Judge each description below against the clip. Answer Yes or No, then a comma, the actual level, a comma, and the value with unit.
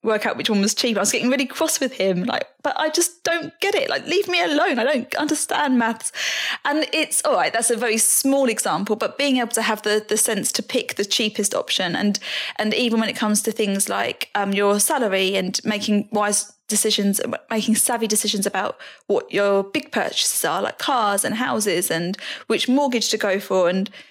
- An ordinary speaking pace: No, fast, 215 wpm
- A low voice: No, high, 225 Hz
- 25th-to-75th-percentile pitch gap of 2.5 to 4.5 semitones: No, average, 4.9 semitones